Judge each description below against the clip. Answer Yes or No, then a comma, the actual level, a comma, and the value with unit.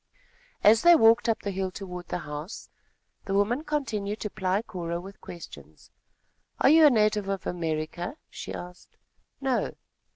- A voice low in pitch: No, high, 200 Hz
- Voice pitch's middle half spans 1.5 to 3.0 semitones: No, average, 4.2 semitones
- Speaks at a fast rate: No, average, 155 wpm